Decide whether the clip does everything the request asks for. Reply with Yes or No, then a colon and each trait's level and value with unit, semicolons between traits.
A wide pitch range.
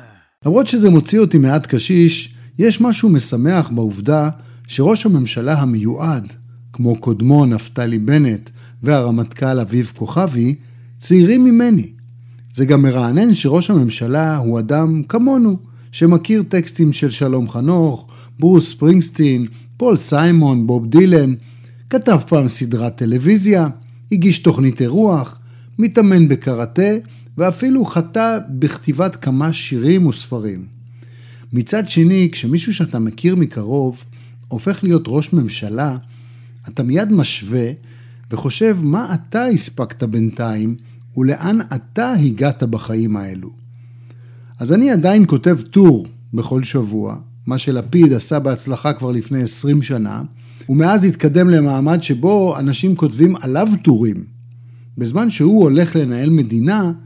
Yes: wide, 6.1 semitones